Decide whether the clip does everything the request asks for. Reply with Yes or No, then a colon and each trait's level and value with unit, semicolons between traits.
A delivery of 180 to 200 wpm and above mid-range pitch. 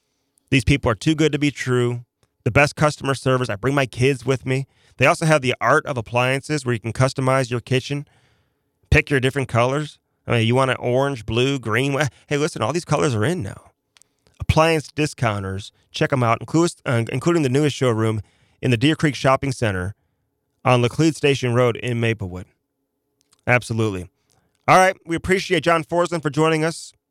No: average, 185 wpm; low, 135 Hz